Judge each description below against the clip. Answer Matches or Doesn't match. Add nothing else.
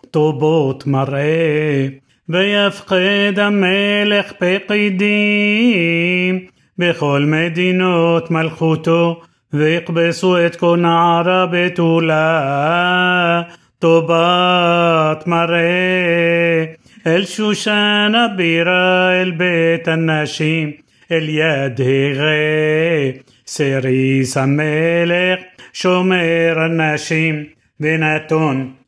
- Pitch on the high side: Doesn't match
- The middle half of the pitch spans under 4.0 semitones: Matches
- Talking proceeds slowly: Matches